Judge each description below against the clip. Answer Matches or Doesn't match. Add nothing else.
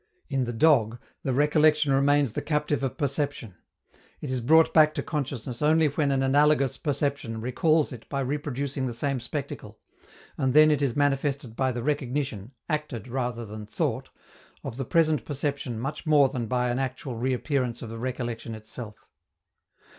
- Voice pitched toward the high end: Doesn't match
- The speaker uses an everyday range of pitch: Matches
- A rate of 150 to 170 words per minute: Matches